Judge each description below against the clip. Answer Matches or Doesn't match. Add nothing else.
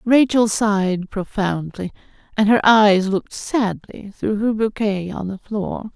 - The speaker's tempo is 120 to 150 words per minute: Matches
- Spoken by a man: Doesn't match